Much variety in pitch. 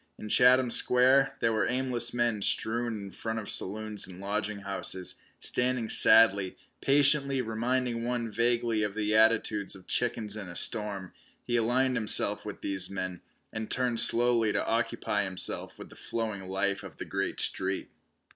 No: average, 3.2 semitones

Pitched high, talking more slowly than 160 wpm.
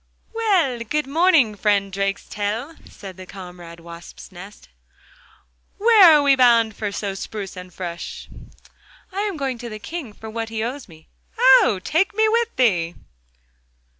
Yes: high, 225 Hz; average, 145 wpm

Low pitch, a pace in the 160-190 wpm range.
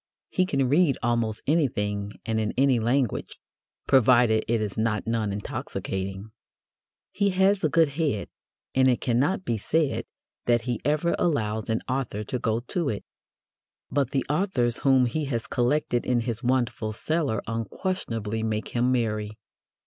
No: low, 120 Hz; average, 150 wpm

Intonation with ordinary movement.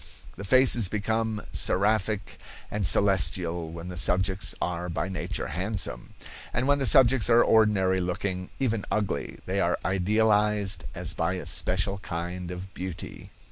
Yes: average, 3.0 semitones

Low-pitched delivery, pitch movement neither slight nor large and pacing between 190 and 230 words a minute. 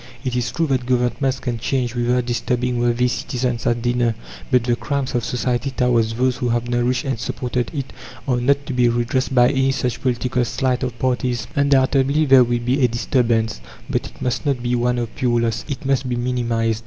No: low, 125 Hz; narrow, 1.5 semitones; fast, 205 wpm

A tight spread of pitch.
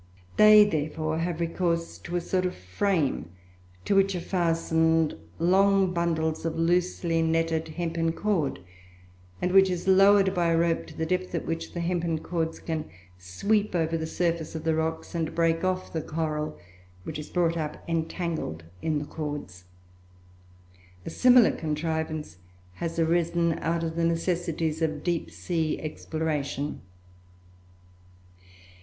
Yes: narrow, 1.7 semitones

